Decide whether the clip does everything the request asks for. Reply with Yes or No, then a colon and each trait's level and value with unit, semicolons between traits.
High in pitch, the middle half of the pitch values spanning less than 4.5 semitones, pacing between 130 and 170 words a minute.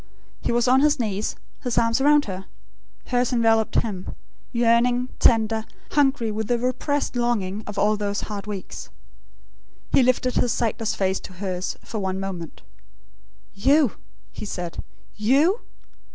Yes: high, 225 Hz; average, 3.7 semitones; average, 140 wpm